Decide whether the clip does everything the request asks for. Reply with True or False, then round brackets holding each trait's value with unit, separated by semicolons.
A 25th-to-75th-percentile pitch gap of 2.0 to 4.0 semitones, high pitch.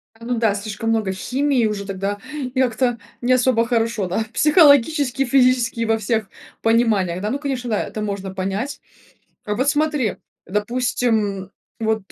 True (3.5 semitones; 230 Hz)